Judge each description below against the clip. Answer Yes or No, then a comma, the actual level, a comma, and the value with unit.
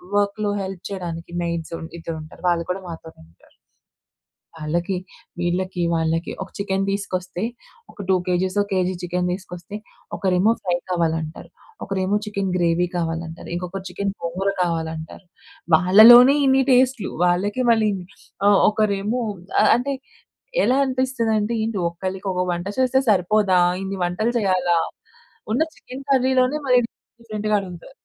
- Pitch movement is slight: No, average, 3.5 semitones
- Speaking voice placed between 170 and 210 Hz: Yes, high, 190 Hz